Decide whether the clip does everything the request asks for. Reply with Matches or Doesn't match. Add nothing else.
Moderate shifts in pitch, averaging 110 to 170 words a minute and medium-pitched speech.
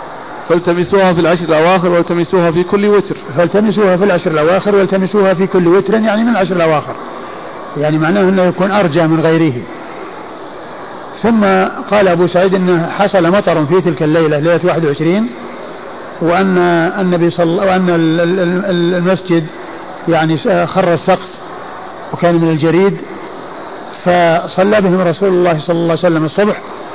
Doesn't match